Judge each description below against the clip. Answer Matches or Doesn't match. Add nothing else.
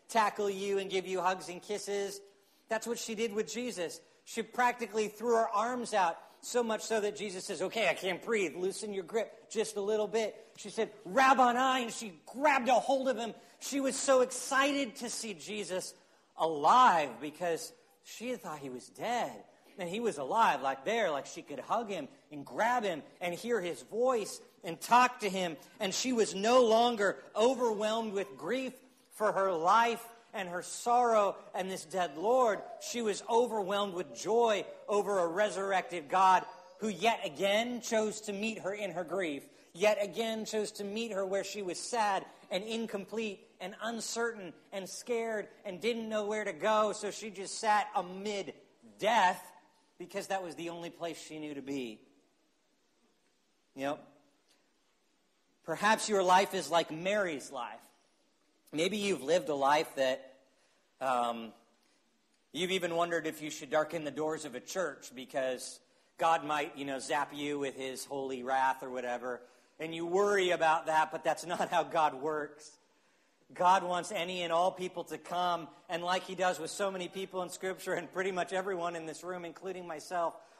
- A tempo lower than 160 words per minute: Doesn't match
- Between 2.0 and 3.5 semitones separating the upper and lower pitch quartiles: Doesn't match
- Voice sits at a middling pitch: Doesn't match